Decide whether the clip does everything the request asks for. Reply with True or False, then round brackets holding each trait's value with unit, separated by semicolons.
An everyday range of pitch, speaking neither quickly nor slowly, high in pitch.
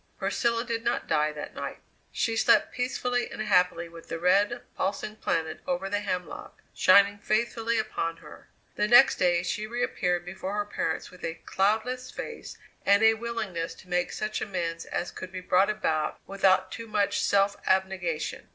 True (3.8 semitones; 170 wpm; 200 Hz)